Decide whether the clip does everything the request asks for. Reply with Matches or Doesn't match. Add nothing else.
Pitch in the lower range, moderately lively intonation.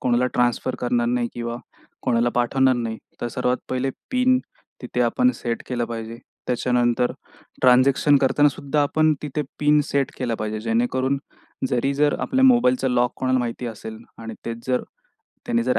Matches